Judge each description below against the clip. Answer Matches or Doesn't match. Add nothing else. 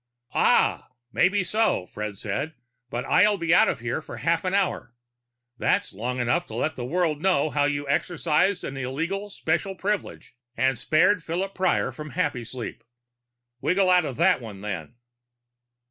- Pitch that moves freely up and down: Matches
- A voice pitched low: Doesn't match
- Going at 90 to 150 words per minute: Doesn't match